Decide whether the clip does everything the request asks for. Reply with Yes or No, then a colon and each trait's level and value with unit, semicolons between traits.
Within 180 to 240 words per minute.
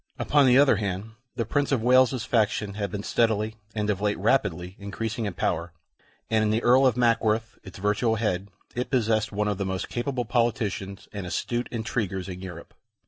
Yes: average, 190 wpm